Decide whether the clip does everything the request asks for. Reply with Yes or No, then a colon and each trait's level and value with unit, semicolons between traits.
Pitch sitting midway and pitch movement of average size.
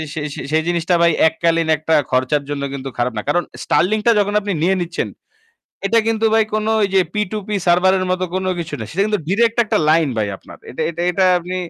Yes: medium, 175 Hz; average, 4.3 semitones